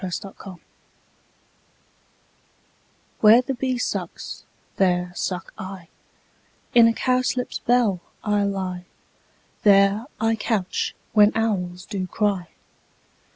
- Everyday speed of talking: No, slow, 105 wpm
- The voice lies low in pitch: No, high, 200 Hz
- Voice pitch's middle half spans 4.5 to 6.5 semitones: No, average, 3.5 semitones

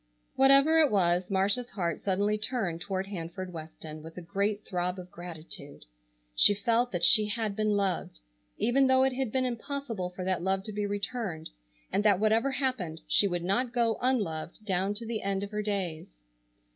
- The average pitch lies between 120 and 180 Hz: No, high, 200 Hz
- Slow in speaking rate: No, average, 185 wpm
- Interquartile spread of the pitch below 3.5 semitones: No, average, 4.5 semitones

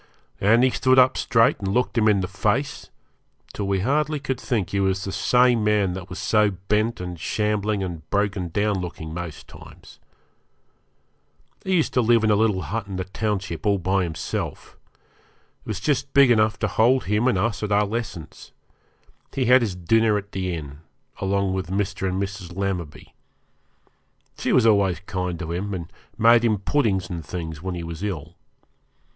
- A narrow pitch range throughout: No, average, 3.5 semitones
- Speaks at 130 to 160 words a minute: No, average, 185 wpm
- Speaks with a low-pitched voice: Yes, low, 100 Hz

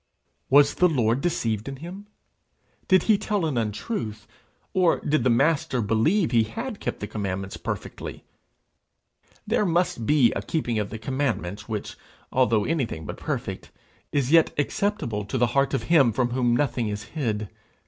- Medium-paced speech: Yes, average, 160 wpm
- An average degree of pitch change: No, wide, 6.7 semitones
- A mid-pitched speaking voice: No, low, 130 Hz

